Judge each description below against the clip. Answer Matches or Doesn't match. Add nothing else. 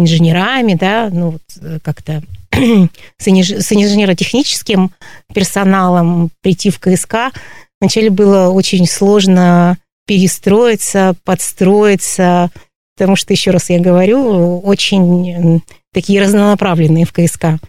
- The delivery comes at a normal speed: Doesn't match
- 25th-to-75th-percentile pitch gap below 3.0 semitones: Matches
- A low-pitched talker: Doesn't match